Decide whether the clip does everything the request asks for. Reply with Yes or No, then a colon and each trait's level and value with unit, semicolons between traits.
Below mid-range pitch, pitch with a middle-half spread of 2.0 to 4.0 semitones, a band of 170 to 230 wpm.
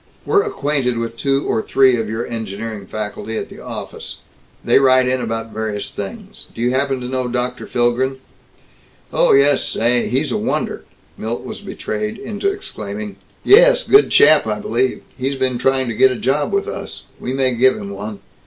Yes: low, 125 Hz; average, 3.4 semitones; average, 180 wpm